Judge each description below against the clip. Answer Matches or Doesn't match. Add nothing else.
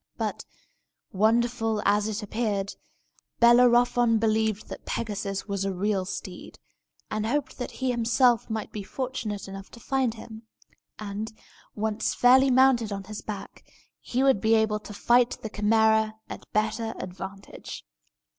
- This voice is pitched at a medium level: Doesn't match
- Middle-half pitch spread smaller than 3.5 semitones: Matches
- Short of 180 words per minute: Matches